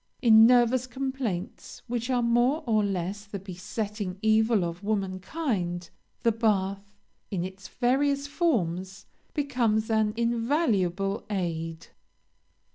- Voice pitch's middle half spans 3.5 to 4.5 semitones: Yes, average, 4.2 semitones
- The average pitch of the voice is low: No, high, 215 Hz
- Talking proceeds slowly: Yes, slow, 110 wpm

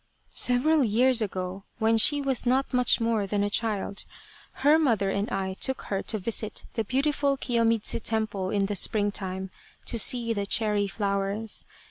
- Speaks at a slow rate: No, average, 165 wpm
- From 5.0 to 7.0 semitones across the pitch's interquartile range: No, average, 3.7 semitones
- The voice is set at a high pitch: Yes, high, 220 Hz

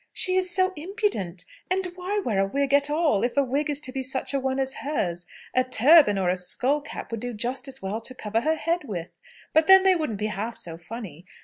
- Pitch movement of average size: No, wide, 6.8 semitones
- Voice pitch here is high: Yes, very high, 265 Hz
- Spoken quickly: Yes, fast, 240 wpm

